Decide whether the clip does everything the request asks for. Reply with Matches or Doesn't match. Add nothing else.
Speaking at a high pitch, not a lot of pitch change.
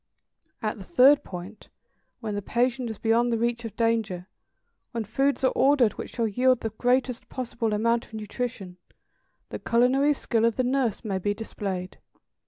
Doesn't match